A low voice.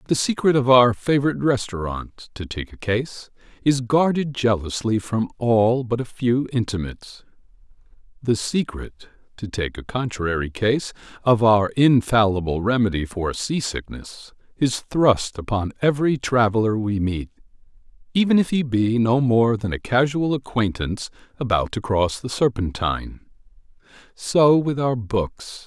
Yes: low, 115 Hz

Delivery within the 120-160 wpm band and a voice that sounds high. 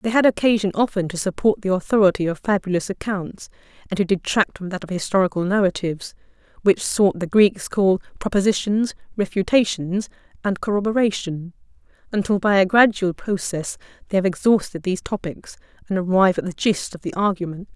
Yes: average, 155 wpm; high, 195 Hz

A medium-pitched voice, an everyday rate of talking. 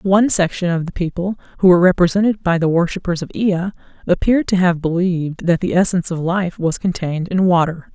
Yes: medium, 180 Hz; average, 195 wpm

